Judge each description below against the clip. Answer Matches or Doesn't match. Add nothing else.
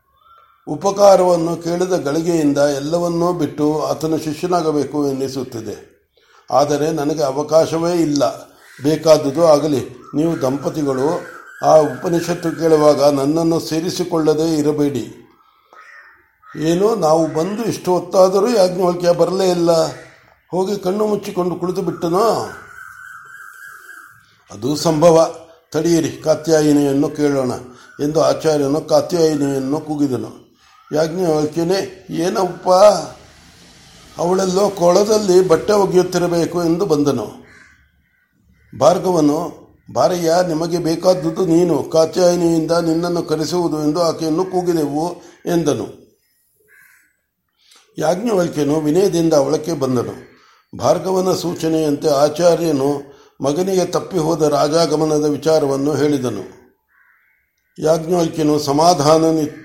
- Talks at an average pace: Matches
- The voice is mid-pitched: Matches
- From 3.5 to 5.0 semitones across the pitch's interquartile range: Doesn't match